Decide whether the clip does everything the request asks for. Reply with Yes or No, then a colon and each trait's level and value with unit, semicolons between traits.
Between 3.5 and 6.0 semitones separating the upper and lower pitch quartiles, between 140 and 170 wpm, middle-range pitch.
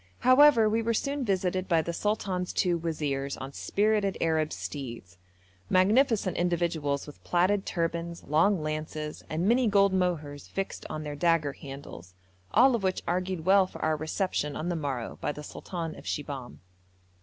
Yes: average, 4.5 semitones; average, 160 wpm; medium, 170 Hz